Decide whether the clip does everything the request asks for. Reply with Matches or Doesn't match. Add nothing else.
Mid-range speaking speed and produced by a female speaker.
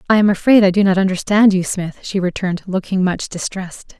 Doesn't match